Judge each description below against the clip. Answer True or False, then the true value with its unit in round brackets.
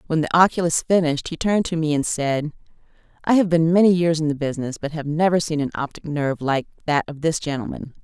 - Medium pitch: True (155 Hz)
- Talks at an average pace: False (225 wpm)